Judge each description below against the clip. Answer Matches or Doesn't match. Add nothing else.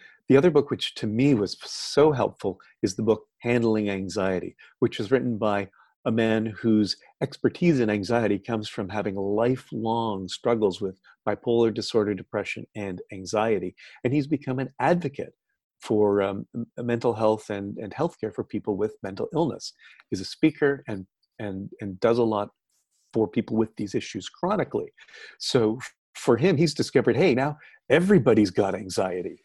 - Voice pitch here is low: Matches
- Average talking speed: Matches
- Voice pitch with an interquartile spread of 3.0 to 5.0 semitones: Doesn't match